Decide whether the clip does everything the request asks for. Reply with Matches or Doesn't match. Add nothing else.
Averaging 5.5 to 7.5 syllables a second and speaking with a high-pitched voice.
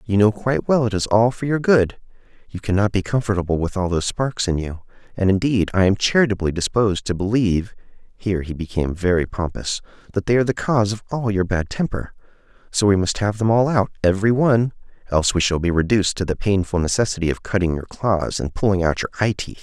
Doesn't match